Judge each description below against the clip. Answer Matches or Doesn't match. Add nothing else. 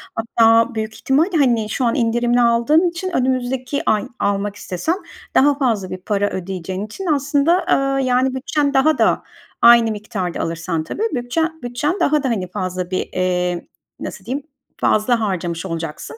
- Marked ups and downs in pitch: Matches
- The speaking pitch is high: Matches